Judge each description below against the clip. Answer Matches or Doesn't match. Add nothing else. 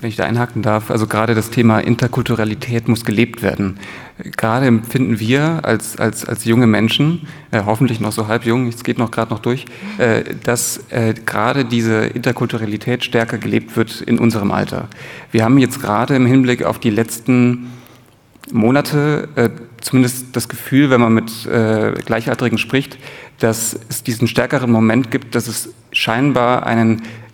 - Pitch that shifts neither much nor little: Doesn't match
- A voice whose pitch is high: Doesn't match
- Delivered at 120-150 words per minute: Doesn't match